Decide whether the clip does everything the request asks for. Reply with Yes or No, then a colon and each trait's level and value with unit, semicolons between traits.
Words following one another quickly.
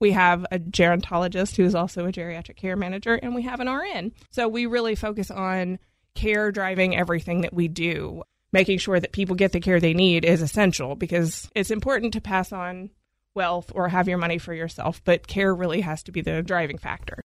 Yes: fast, 210 wpm